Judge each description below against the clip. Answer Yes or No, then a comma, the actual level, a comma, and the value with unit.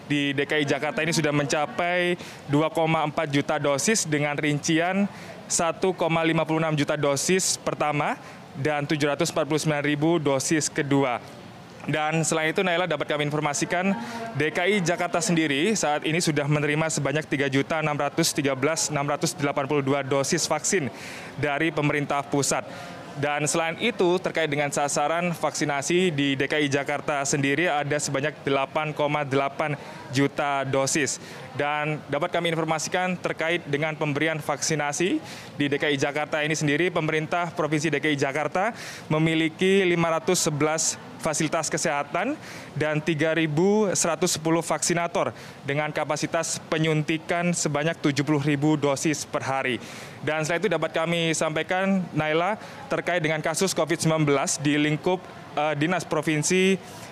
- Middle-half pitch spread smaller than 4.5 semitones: Yes, narrow, 2.4 semitones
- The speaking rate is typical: Yes, average, 110 wpm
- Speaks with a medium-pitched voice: Yes, medium, 155 Hz